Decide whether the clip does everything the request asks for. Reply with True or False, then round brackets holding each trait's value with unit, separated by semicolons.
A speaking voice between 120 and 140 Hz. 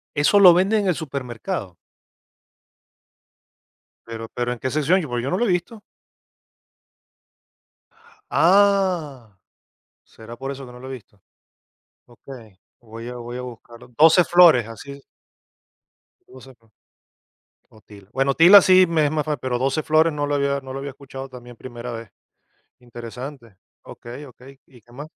True (135 Hz)